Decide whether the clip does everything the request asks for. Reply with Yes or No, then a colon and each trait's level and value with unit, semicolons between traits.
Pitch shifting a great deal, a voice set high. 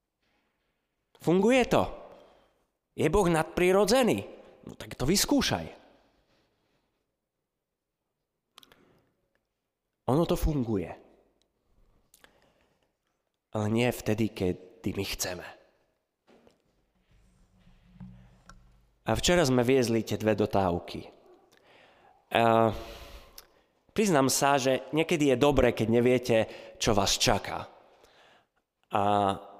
No: wide, 6.3 semitones; low, 115 Hz